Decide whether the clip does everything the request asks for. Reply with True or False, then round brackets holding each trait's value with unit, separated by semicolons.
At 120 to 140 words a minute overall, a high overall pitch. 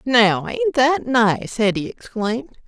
True (135 wpm; 220 Hz)